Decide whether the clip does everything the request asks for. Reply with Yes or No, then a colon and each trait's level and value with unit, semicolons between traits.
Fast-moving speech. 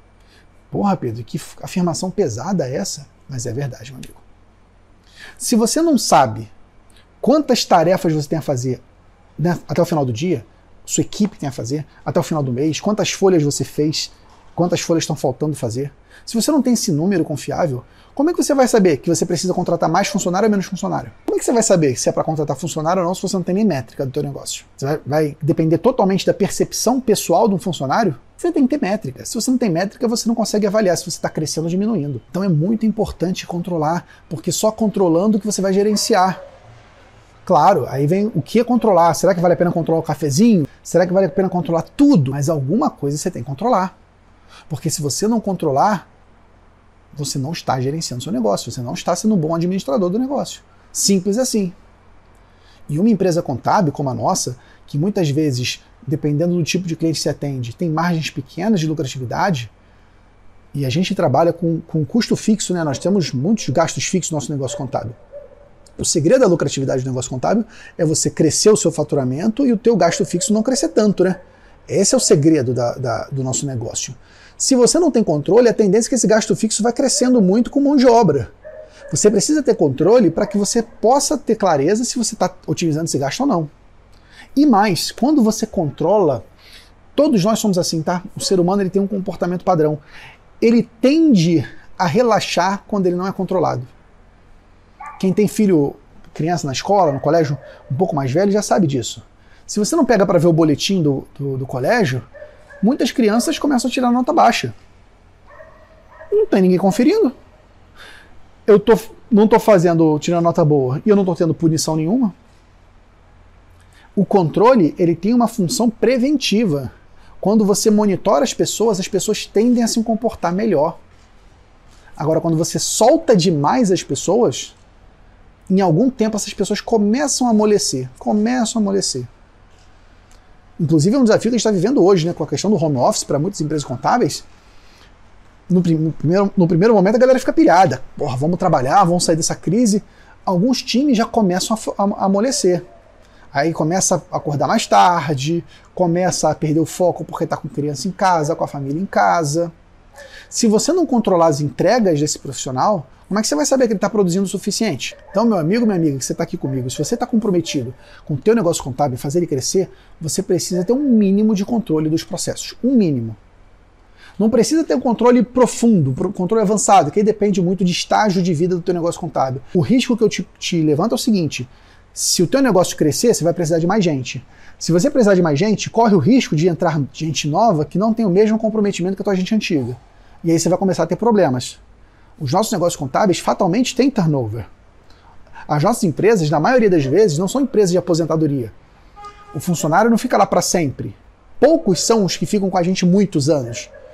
Yes: fast, 195 wpm